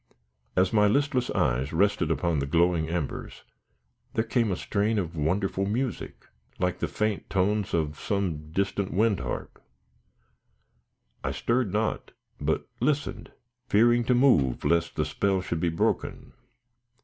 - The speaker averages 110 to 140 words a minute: Yes, slow, 135 wpm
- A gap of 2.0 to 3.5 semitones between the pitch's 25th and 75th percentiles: No, average, 4.7 semitones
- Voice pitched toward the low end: Yes, very low, 95 Hz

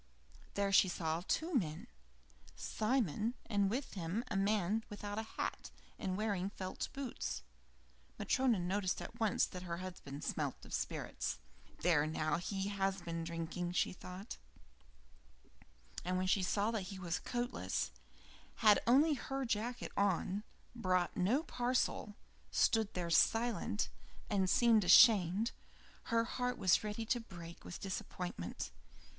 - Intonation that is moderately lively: Yes, average, 4.3 semitones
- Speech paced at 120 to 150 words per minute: Yes, slow, 135 wpm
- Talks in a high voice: Yes, high, 195 Hz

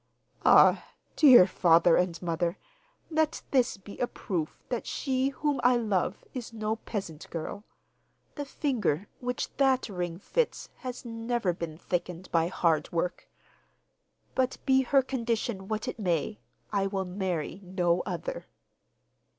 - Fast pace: No, slow, 135 wpm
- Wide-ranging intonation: Yes, wide, 6.2 semitones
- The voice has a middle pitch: No, high, 205 Hz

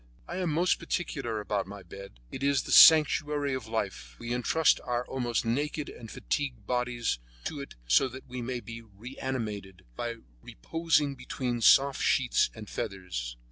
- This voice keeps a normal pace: Yes, average, 160 wpm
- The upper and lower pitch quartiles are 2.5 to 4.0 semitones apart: No, average, 4.8 semitones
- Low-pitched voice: Yes, low, 120 Hz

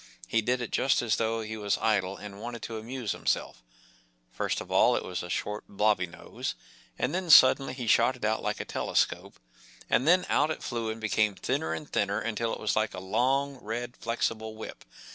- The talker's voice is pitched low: Yes, low, 110 Hz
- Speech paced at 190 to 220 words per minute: Yes, fast, 205 wpm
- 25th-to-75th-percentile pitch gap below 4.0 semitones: Yes, average, 2.9 semitones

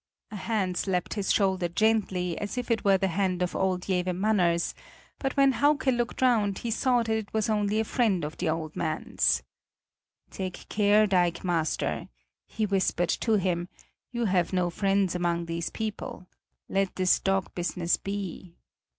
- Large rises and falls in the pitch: No, average, 3.4 semitones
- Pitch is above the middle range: Yes, high, 195 Hz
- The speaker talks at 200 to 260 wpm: No, average, 165 wpm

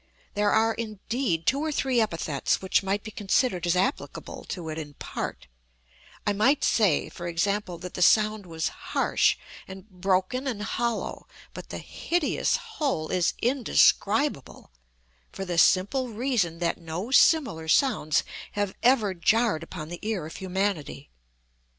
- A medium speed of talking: Yes, average, 145 wpm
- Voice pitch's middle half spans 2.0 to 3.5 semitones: No, average, 5.2 semitones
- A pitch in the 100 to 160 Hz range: No, high, 200 Hz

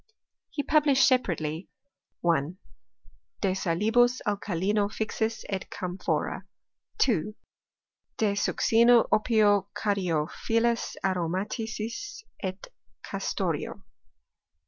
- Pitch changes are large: No, average, 3.8 semitones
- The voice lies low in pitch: No, high, 210 Hz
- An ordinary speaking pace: No, slow, 75 wpm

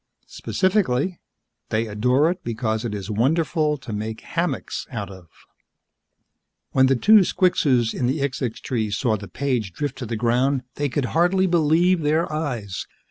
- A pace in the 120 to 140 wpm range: No, average, 155 wpm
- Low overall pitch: Yes, low, 130 Hz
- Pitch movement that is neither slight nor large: No, wide, 5.9 semitones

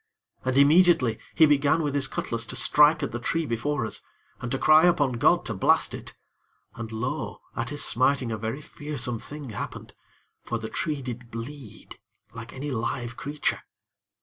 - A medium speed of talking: Yes, average, 175 wpm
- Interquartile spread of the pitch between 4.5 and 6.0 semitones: No, average, 4.1 semitones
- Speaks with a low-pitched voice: Yes, low, 130 Hz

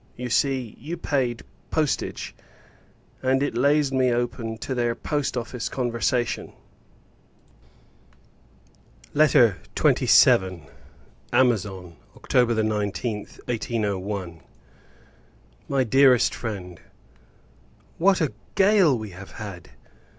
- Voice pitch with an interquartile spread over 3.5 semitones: Yes, average, 4.2 semitones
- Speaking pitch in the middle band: No, low, 120 Hz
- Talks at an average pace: No, slow, 90 wpm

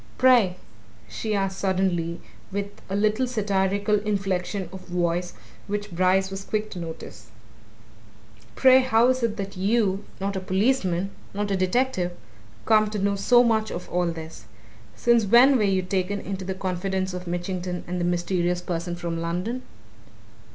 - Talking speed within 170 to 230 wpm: No, average, 160 wpm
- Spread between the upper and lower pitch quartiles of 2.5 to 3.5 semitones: Yes, average, 2.9 semitones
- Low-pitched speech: No, high, 195 Hz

